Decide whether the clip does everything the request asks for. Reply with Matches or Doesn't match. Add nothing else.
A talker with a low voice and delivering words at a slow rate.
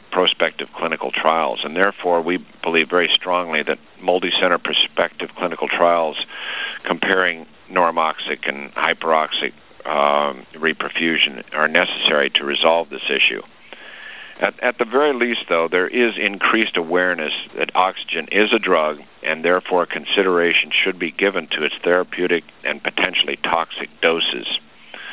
Matches